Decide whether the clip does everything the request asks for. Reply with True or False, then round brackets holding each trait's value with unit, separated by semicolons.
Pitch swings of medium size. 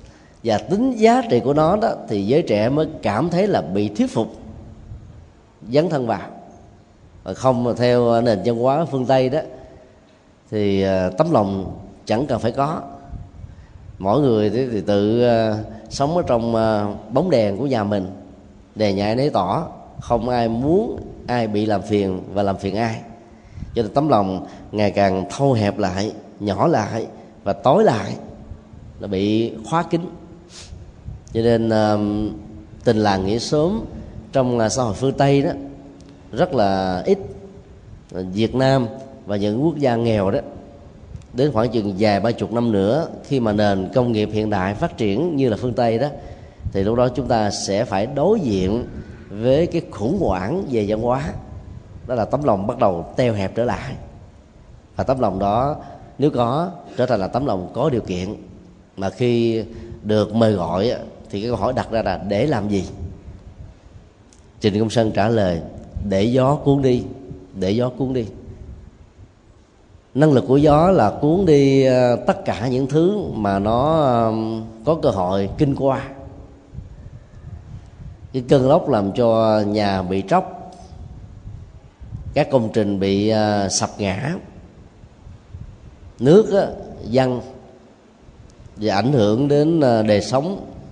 True (4.7 semitones)